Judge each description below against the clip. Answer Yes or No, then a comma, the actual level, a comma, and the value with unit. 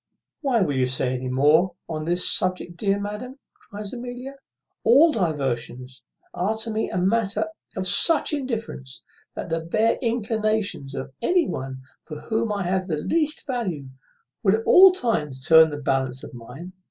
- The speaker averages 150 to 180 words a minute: Yes, average, 160 wpm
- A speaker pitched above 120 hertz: Yes, medium, 185 Hz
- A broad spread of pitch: Yes, wide, 7.7 semitones